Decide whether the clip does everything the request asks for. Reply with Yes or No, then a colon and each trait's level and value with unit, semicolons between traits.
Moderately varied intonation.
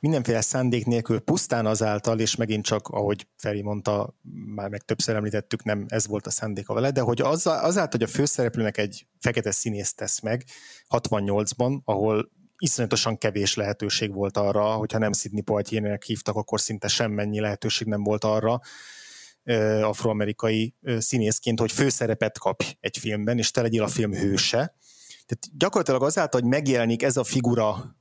No: narrow, 2.3 semitones